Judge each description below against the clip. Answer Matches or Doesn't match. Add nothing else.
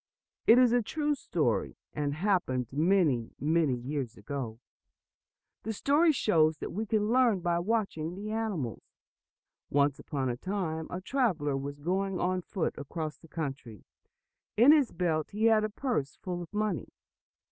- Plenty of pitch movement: Matches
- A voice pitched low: Doesn't match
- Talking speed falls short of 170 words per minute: Matches